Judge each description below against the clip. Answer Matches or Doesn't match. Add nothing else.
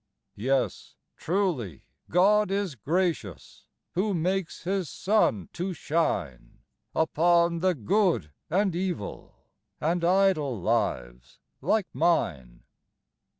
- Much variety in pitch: Matches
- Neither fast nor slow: Doesn't match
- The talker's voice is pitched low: Doesn't match